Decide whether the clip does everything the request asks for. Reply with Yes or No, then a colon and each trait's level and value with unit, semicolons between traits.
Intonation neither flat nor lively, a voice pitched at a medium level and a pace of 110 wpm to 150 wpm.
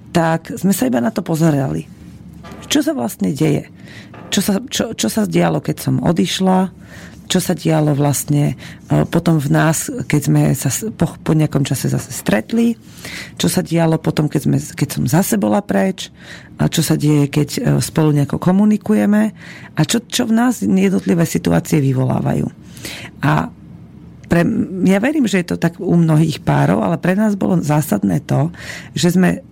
No: average, 4.8 semitones; medium, 165 Hz; fast, 165 wpm